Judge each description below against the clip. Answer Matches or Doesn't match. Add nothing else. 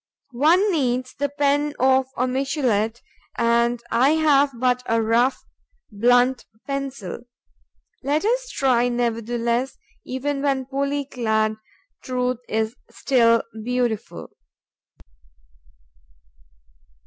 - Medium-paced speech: Doesn't match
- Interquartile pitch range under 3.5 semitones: Matches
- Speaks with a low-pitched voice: Doesn't match